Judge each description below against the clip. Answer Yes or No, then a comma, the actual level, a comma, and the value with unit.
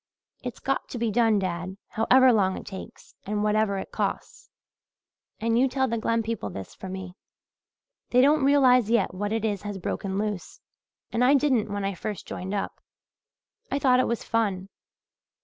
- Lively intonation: No, average, 4.1 semitones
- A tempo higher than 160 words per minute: Yes, average, 175 wpm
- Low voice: No, high, 220 Hz